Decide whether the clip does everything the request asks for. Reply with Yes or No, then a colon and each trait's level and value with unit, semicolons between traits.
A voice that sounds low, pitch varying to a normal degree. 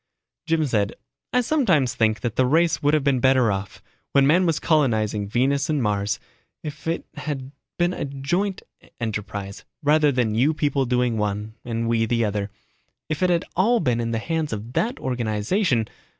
No: low, 130 Hz; wide, 5.8 semitones